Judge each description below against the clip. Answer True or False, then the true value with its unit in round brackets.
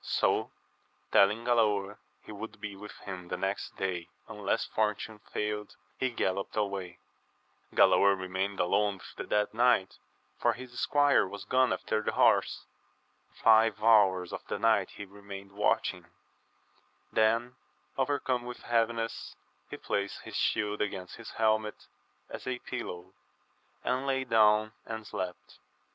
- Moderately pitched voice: False (105 Hz)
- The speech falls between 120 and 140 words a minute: True (135 wpm)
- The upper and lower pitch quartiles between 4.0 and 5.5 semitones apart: False (2.7 semitones)